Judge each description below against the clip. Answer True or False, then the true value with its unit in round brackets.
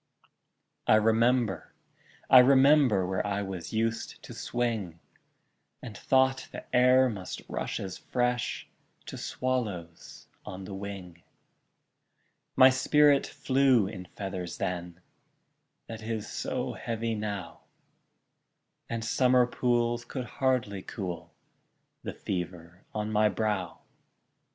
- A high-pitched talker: False (110 Hz)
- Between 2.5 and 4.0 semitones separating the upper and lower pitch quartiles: False (4.7 semitones)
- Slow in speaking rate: True (110 wpm)